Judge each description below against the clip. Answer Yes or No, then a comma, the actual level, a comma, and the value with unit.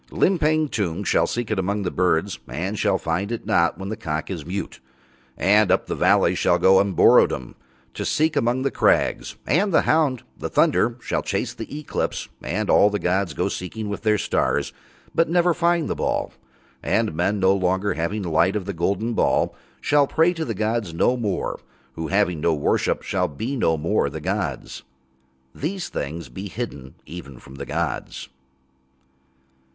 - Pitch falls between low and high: No, low, 100 Hz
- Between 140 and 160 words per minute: No, average, 175 wpm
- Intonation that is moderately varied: No, wide, 5.8 semitones